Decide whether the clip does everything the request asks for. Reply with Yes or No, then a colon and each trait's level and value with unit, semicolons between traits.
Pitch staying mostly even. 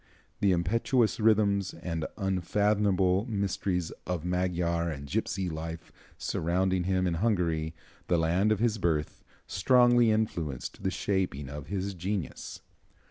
No: average, 3.4 semitones